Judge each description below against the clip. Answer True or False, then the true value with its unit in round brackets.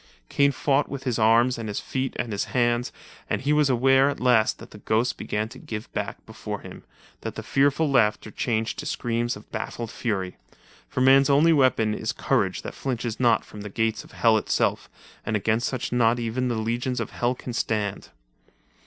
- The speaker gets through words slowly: False (195 wpm)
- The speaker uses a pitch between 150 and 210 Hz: False (120 Hz)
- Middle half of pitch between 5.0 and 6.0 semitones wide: False (3.0 semitones)